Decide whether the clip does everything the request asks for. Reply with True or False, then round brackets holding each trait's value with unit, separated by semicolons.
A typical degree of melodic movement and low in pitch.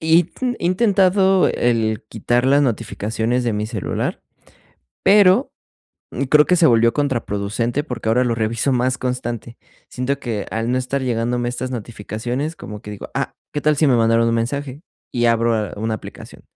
True (4.0 semitones; 120 Hz)